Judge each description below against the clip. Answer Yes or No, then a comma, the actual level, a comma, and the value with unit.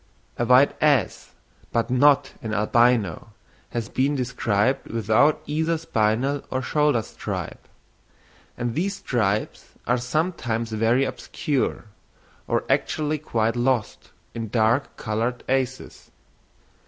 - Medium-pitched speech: No, low, 125 Hz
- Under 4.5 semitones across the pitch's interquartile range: Yes, average, 4.0 semitones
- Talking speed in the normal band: No, slow, 110 wpm